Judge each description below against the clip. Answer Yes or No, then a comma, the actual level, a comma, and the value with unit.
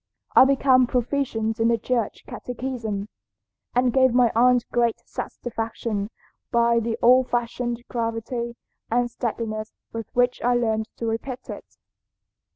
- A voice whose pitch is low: No, high, 235 Hz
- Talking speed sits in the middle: No, slow, 130 wpm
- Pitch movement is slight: Yes, narrow, 1.6 semitones